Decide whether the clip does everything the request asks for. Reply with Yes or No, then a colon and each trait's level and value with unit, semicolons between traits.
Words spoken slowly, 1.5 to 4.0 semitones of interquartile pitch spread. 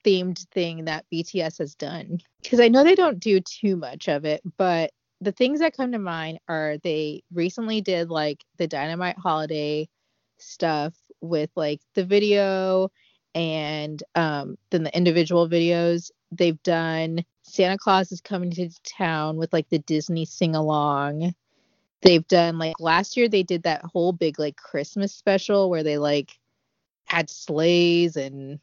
No: average, 155 wpm; average, 3.2 semitones